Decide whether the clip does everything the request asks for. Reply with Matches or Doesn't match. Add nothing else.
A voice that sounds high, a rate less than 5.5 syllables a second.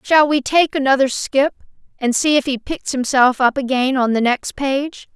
Matches